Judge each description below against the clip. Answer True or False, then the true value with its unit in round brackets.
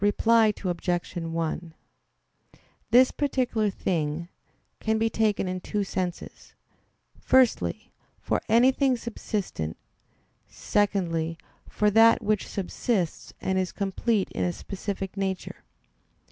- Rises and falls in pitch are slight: False (4.2 semitones)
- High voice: True (195 Hz)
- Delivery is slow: True (105 wpm)